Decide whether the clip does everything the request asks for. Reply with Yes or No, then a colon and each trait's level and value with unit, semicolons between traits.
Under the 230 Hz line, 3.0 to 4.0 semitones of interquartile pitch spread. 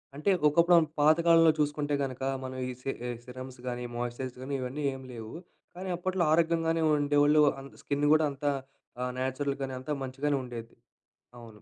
Yes: medium, 140 Hz; average, 3.3 semitones